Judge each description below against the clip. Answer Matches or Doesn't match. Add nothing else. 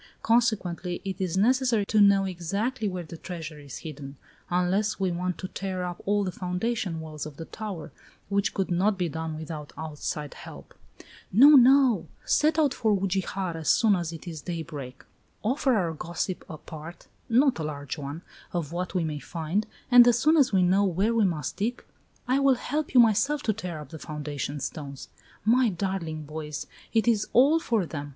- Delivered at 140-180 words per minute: Doesn't match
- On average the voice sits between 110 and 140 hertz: Doesn't match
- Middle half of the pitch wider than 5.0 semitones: Matches